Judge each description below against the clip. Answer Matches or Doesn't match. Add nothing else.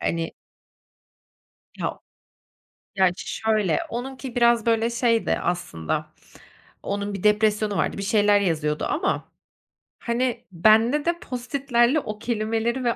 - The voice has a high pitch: Matches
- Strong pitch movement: Doesn't match